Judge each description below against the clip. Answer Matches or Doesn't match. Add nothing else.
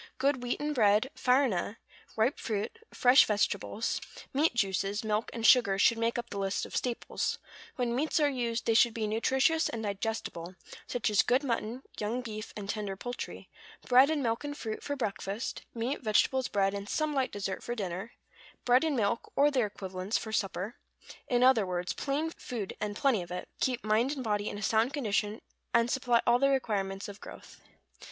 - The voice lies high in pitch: Matches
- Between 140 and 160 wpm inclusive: Doesn't match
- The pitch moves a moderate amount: Matches